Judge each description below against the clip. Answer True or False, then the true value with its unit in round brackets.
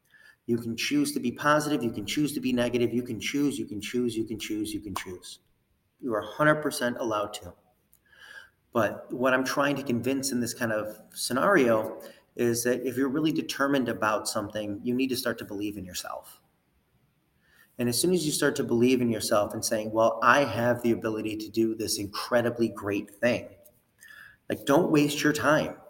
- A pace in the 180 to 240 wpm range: True (195 wpm)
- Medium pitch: False (120 Hz)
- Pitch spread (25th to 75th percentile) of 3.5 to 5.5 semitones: True (4.3 semitones)